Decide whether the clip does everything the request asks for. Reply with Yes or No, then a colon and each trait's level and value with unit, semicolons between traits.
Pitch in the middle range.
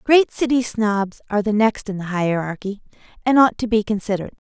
No: high, 215 Hz